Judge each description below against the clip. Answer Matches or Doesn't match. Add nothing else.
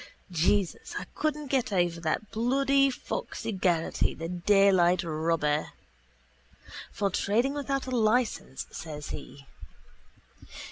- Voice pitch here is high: Matches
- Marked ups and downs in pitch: Matches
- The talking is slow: Matches